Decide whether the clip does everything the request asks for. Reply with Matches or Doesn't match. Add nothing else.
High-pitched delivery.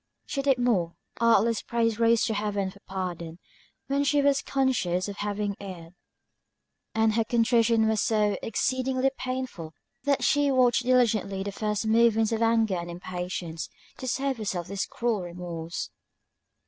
Matches